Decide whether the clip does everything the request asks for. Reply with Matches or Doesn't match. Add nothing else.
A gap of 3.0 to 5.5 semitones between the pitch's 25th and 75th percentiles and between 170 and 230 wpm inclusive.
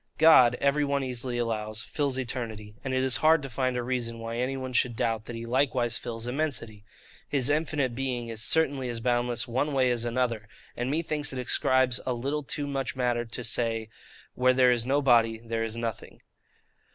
Doesn't match